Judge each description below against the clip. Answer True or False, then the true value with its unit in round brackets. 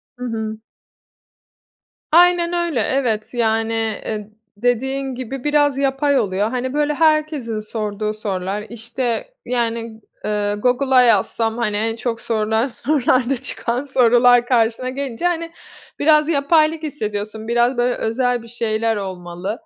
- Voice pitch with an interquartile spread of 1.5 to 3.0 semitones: False (3.7 semitones)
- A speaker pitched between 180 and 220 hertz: False (240 Hz)